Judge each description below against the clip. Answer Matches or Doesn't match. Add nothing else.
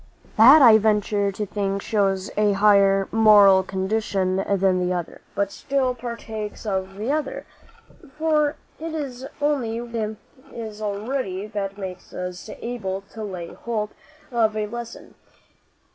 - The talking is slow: Doesn't match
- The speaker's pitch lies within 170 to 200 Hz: Doesn't match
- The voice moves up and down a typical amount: Matches